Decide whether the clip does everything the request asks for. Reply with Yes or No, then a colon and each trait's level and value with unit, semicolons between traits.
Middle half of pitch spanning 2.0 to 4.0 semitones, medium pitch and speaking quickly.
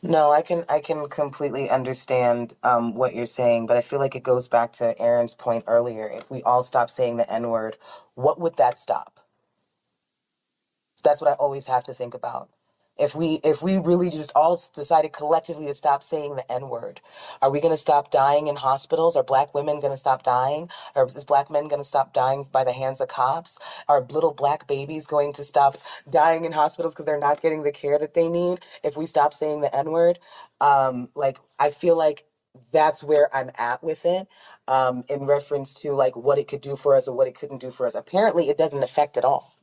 Yes: average, 3.1 semitones; medium, 145 Hz; fast, 215 wpm